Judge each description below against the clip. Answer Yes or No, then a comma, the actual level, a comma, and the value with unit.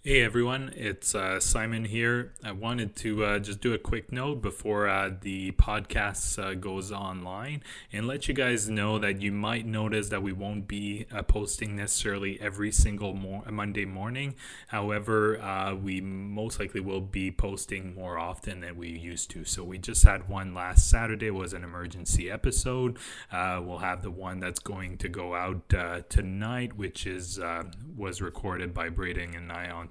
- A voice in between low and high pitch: No, low, 100 Hz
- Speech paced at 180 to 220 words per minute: Yes, average, 185 wpm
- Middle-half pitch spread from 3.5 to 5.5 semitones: No, average, 2.9 semitones